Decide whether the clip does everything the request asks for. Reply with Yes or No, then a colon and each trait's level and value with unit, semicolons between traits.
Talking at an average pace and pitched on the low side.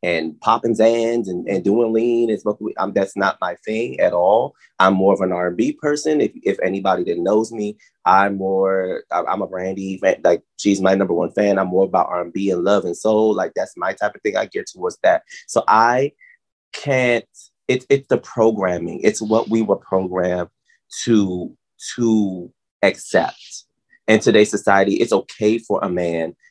Yes: average, 185 wpm; low, 105 Hz